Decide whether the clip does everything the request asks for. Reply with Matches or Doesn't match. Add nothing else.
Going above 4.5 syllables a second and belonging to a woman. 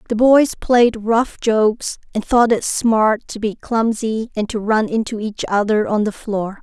Doesn't match